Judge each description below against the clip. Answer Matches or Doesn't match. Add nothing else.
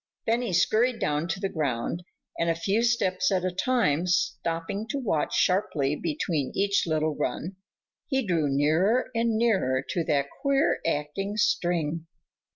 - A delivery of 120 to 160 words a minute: Matches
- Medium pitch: Matches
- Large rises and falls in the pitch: Matches